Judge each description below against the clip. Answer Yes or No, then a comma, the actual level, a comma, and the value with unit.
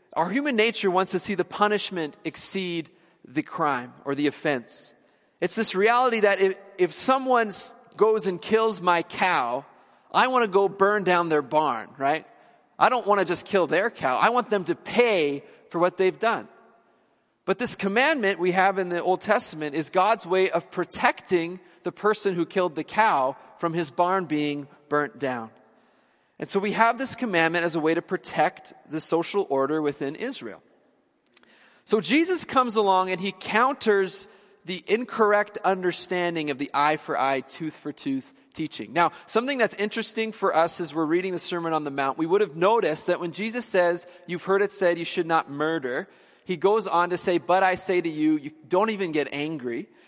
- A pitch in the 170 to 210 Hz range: Yes, medium, 185 Hz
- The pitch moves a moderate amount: Yes, average, 4.4 semitones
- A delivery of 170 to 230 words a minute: Yes, average, 190 wpm